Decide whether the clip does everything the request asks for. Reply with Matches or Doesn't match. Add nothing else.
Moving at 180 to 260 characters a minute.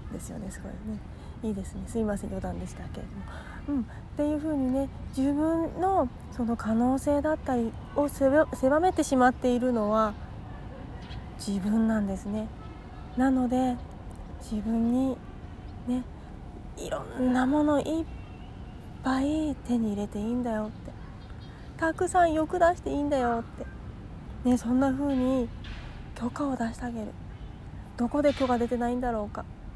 Doesn't match